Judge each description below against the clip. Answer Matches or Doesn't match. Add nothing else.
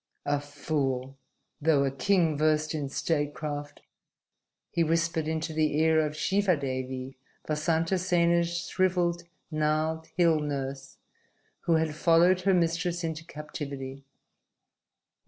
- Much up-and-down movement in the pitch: Doesn't match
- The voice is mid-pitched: Matches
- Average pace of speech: Doesn't match